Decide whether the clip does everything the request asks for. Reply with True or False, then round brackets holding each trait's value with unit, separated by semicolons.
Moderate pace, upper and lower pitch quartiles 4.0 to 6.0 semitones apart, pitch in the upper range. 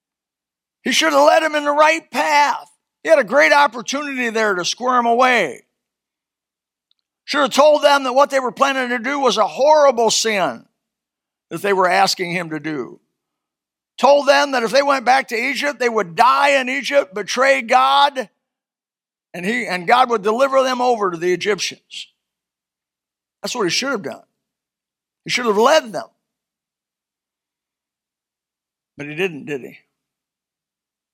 True (160 wpm; 4.5 semitones; 255 Hz)